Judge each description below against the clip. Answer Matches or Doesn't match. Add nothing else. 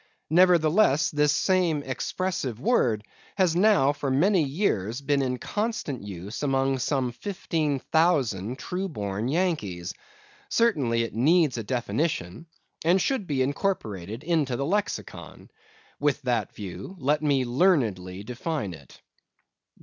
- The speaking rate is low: Matches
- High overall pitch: Doesn't match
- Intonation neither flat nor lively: Doesn't match